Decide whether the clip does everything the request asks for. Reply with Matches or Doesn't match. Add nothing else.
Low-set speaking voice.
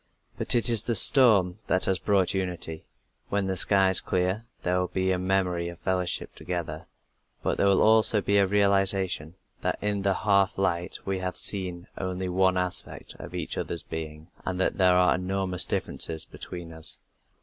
Matches